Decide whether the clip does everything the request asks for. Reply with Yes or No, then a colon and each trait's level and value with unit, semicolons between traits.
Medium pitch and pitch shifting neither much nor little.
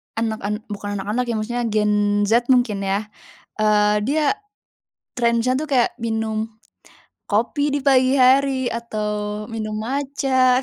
No: high, 230 Hz; average, 3.5 semitones